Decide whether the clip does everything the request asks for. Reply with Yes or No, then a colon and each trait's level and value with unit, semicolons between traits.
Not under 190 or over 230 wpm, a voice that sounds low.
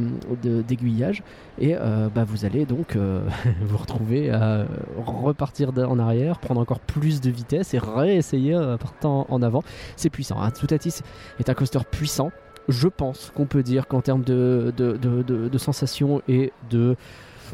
No: average, 175 wpm; low, 125 Hz